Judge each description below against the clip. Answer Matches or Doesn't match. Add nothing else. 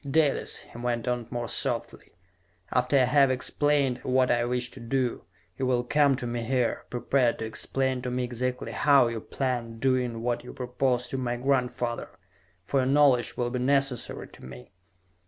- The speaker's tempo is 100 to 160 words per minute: Doesn't match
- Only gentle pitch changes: Matches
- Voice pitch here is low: Matches